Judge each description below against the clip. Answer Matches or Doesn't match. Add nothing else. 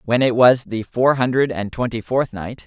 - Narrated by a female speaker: Doesn't match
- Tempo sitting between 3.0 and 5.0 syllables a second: Matches